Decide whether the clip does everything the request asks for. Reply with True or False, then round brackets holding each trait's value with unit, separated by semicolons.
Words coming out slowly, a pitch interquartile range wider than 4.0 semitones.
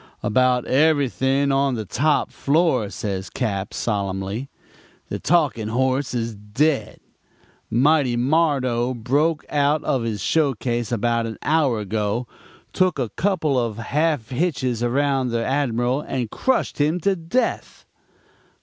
True (125 wpm; 4.4 semitones)